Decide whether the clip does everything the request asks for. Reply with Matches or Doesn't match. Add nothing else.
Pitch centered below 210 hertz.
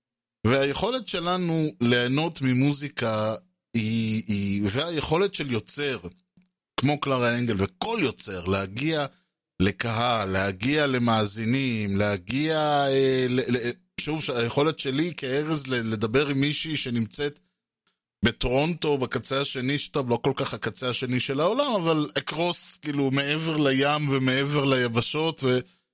Matches